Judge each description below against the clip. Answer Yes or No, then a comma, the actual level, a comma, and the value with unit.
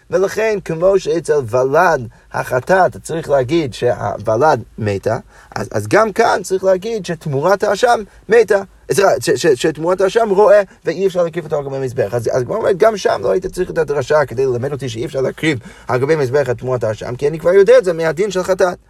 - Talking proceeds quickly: Yes, fast, 185 wpm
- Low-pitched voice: No, medium, 170 Hz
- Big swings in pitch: Yes, wide, 6.4 semitones